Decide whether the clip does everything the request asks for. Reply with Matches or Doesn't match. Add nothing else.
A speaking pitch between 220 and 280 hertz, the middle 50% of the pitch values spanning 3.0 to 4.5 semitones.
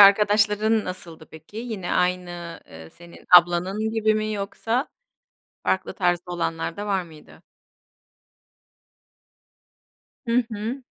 Doesn't match